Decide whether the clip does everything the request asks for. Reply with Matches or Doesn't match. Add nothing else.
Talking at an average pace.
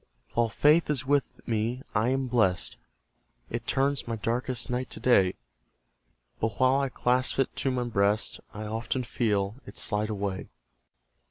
Matches